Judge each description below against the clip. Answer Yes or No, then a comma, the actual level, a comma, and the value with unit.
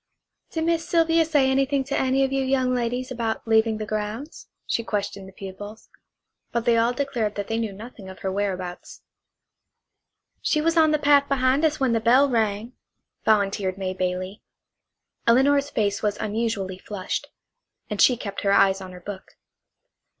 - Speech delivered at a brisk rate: No, average, 170 wpm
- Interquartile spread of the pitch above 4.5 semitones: Yes, average, 5.1 semitones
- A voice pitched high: Yes, high, 225 Hz